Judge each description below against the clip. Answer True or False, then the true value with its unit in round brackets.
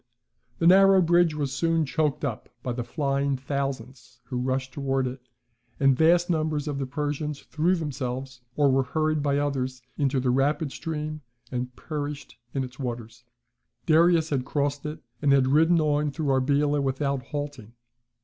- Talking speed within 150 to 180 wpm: True (165 wpm)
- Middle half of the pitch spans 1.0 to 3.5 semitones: True (2.7 semitones)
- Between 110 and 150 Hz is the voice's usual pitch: True (140 Hz)